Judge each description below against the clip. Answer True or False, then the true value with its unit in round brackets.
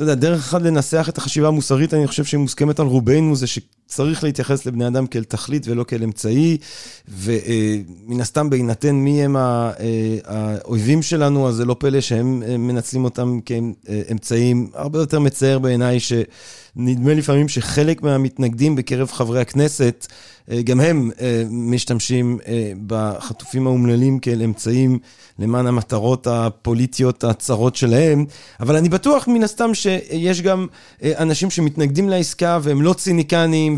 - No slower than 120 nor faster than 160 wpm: True (150 wpm)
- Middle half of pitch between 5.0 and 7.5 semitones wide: False (4.1 semitones)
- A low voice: True (130 Hz)